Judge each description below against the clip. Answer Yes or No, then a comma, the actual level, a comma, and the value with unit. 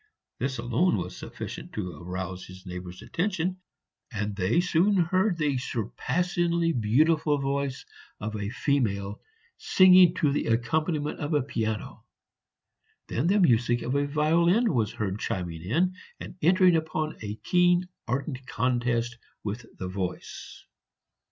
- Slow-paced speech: Yes, slow, 130 wpm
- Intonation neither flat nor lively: No, wide, 7.8 semitones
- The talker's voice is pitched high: No, low, 135 Hz